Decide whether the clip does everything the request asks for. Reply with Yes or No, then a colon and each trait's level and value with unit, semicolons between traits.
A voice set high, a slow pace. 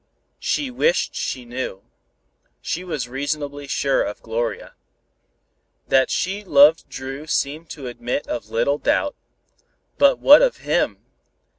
No: medium, 140 Hz; slow, 125 wpm